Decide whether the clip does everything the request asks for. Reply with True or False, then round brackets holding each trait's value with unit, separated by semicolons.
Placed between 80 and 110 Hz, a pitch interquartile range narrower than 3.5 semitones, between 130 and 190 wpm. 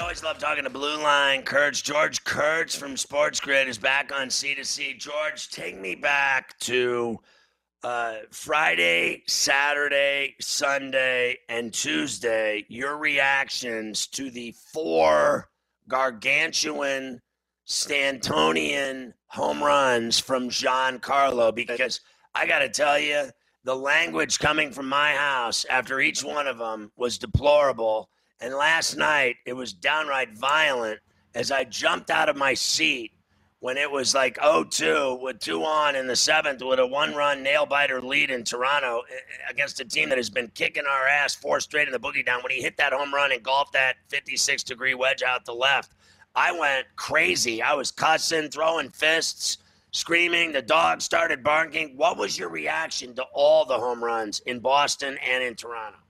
False (135 Hz; 3.0 semitones; 160 wpm)